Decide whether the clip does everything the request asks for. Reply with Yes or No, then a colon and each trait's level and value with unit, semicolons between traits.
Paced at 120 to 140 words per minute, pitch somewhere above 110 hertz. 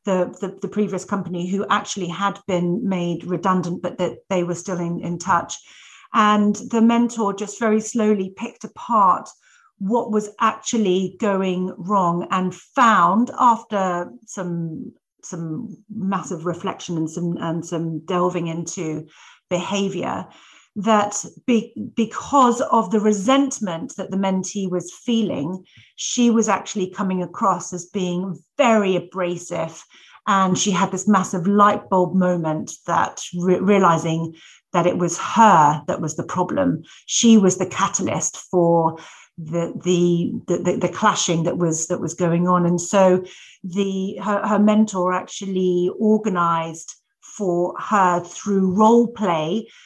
Yes: slow, 135 wpm; high, 190 Hz